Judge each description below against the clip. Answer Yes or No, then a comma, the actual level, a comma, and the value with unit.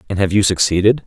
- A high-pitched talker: No, low, 100 Hz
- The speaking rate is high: Yes, fast, 225 wpm